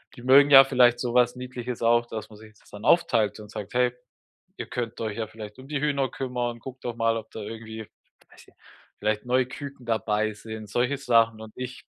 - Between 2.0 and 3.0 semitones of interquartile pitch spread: Yes, narrow, 2.5 semitones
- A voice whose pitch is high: No, low, 120 Hz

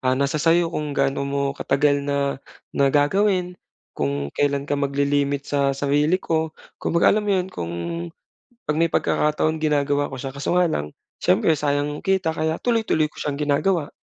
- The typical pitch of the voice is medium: Yes, medium, 145 Hz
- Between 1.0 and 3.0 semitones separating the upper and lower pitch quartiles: Yes, narrow, 2.4 semitones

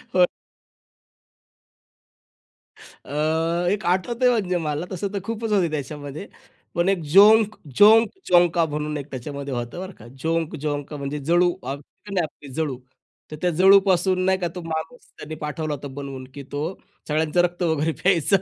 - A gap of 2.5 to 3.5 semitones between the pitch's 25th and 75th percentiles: No, average, 4.2 semitones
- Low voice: No, medium, 165 Hz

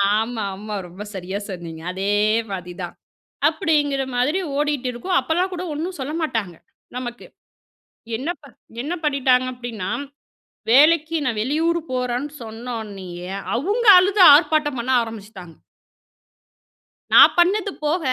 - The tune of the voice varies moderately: No, wide, 6.7 semitones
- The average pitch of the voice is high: Yes, very high, 250 Hz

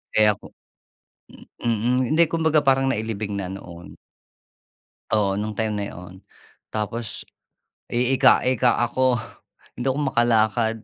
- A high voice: No, low, 115 Hz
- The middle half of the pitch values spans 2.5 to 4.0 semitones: Yes, average, 3.6 semitones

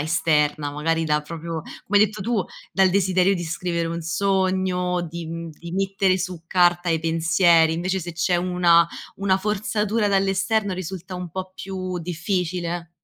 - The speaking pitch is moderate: Yes, medium, 180 Hz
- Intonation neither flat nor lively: No, narrow, 2.3 semitones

